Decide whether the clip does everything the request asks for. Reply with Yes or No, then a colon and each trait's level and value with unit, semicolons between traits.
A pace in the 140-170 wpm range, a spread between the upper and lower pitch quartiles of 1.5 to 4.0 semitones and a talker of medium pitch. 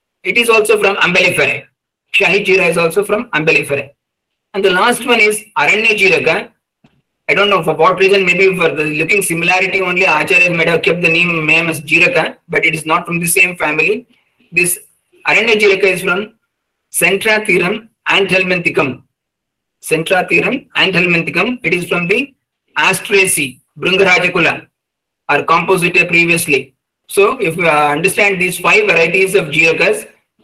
Yes: average, 150 wpm; average, 3.3 semitones; medium, 180 Hz